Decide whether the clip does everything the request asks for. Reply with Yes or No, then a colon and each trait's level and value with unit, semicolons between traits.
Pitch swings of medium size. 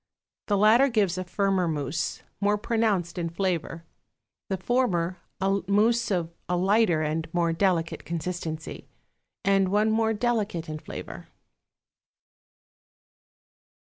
Yes: average, 3.9 semitones